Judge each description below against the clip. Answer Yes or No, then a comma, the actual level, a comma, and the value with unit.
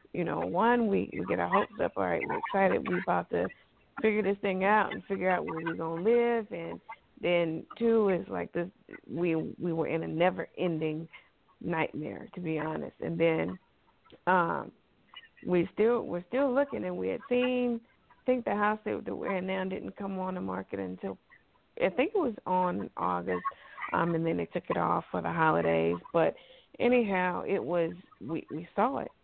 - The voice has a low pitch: No, medium, 185 Hz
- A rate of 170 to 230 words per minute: Yes, average, 195 wpm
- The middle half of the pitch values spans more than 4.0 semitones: Yes, wide, 5.5 semitones